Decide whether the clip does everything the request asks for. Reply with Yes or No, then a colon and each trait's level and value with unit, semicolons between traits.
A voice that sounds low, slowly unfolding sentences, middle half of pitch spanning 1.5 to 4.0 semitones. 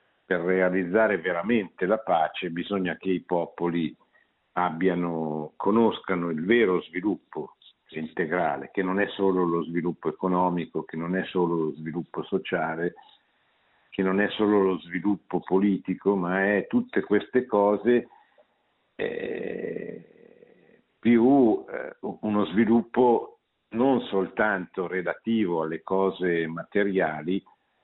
Yes: very low, 95 Hz; slow, 110 wpm; average, 3.3 semitones